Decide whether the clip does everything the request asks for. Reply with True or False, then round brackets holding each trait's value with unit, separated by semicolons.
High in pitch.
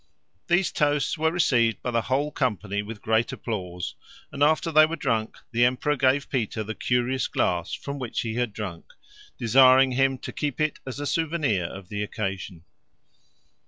False (125 Hz)